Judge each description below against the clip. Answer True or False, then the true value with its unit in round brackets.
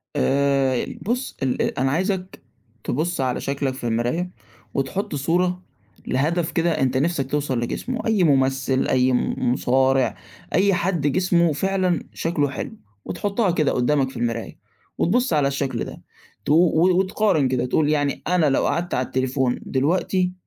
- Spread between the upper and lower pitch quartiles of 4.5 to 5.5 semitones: True (5.2 semitones)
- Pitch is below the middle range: False (145 Hz)